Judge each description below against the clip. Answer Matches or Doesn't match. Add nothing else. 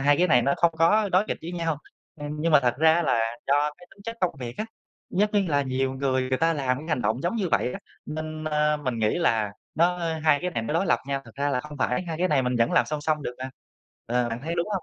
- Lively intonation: Doesn't match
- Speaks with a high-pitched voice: Doesn't match